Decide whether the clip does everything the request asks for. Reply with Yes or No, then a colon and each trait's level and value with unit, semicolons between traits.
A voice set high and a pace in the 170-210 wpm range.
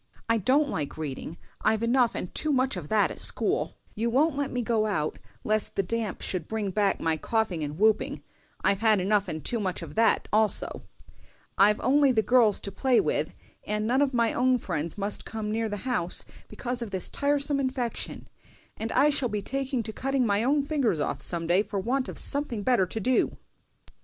Yes: high, 220 Hz; average, 200 wpm